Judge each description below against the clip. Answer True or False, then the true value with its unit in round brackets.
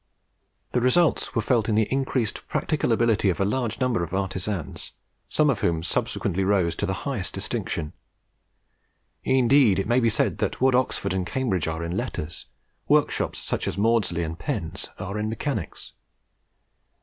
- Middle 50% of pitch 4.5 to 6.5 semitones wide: True (5.2 semitones)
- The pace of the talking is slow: False (160 wpm)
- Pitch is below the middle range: True (105 Hz)